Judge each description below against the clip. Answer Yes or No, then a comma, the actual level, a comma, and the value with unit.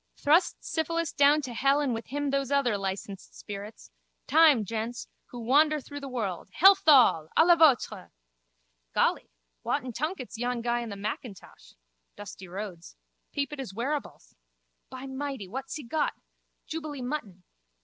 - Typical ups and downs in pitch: Yes, average, 5.0 semitones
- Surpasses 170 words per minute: No, average, 150 wpm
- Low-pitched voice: No, very high, 260 Hz